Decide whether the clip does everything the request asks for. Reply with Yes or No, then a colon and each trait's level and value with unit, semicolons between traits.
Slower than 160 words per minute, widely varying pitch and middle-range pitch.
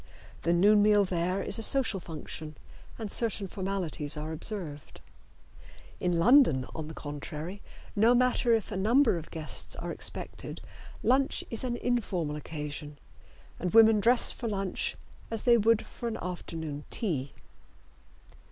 No: average, 145 wpm; wide, 6.1 semitones; high, 195 Hz